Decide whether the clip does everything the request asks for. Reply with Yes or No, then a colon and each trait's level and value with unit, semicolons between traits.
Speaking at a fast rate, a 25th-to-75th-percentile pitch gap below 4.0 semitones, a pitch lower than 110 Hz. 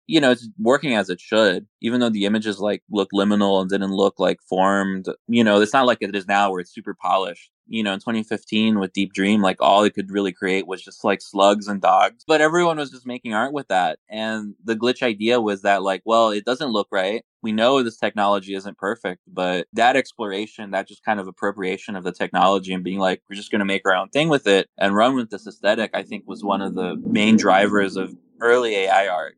Yes: fast, 240 wpm; narrow, 2.4 semitones; low, 100 Hz